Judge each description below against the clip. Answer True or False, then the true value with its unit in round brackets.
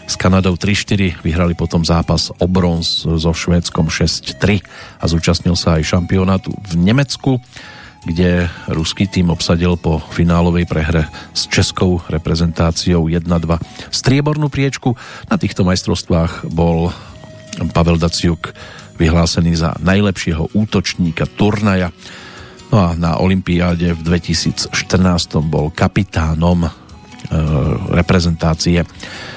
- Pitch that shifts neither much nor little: False (2.2 semitones)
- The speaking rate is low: True (105 wpm)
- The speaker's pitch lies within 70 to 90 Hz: True (85 Hz)